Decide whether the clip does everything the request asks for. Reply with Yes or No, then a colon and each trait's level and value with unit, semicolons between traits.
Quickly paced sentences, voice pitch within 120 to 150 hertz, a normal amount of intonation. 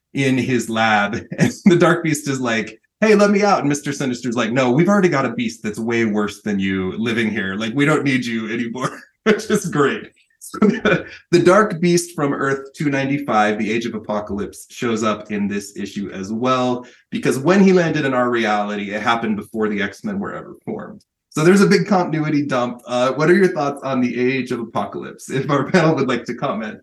No: fast, 215 wpm; low, 130 Hz; wide, 6.4 semitones